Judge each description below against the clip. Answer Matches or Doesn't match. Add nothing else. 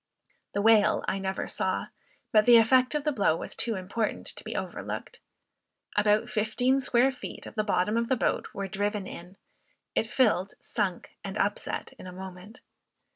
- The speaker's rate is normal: Matches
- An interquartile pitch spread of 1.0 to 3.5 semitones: Matches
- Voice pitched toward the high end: Matches